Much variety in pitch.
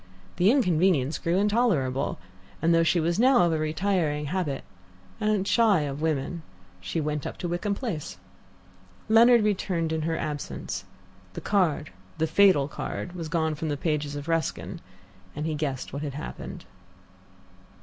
No: average, 4.2 semitones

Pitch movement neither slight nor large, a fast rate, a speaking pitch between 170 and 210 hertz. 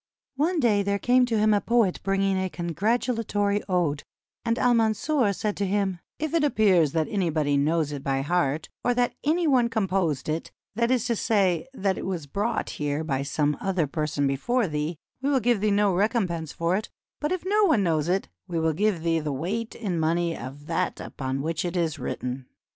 No: wide, 6.2 semitones; fast, 215 wpm; high, 190 Hz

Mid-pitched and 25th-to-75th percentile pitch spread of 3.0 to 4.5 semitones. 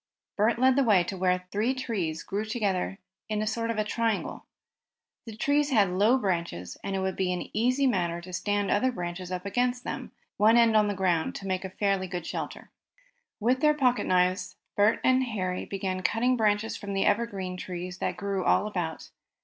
No: high, 205 Hz; average, 4.0 semitones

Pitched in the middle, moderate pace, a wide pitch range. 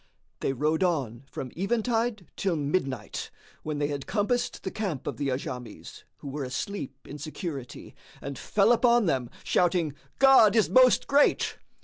Yes: medium, 160 Hz; average, 150 wpm; wide, 7.7 semitones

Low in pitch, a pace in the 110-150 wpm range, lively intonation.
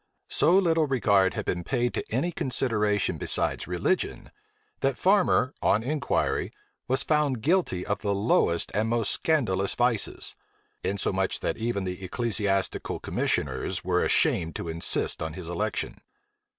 Yes: low, 110 Hz; slow, 135 wpm; wide, 6.0 semitones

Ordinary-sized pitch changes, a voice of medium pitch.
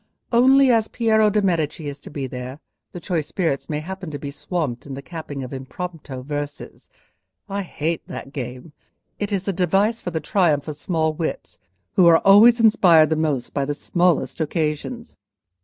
Yes: average, 5.0 semitones; medium, 160 Hz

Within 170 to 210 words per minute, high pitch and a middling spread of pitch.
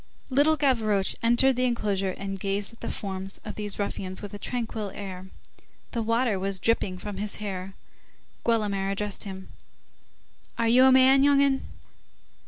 No: average, 160 wpm; high, 210 Hz; average, 3.6 semitones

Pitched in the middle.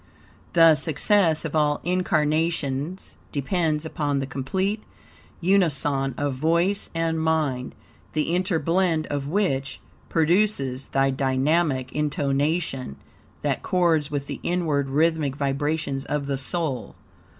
Yes: medium, 150 Hz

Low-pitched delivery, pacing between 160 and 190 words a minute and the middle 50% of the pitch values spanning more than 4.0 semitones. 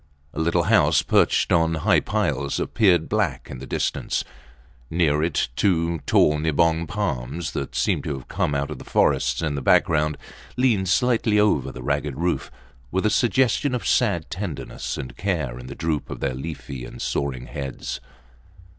Yes: very low, 80 Hz; average, 170 wpm; average, 4.4 semitones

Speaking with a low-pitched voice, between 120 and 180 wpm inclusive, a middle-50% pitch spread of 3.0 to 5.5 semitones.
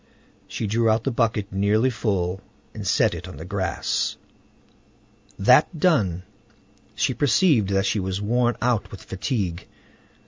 Yes: low, 105 Hz; average, 140 wpm; average, 3.9 semitones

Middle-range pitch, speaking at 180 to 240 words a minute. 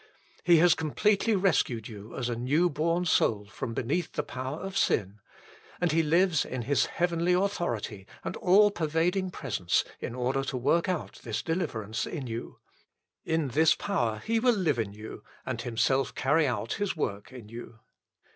No: medium, 150 Hz; average, 170 wpm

